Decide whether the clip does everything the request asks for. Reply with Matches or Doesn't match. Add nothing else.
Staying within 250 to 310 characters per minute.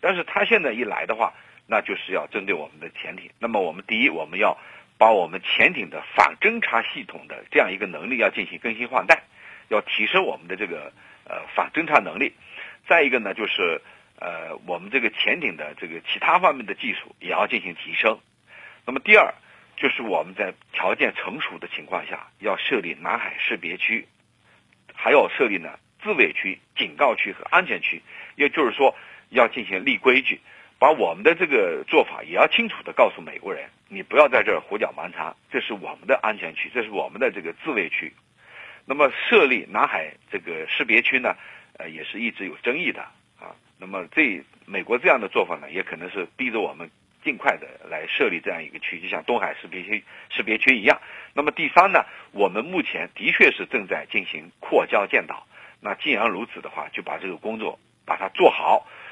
Matches